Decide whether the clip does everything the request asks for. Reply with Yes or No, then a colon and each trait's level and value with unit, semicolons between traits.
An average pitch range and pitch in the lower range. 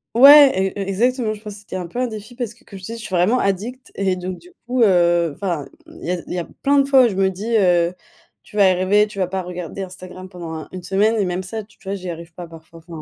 No: average, 3.6 semitones; high, 190 Hz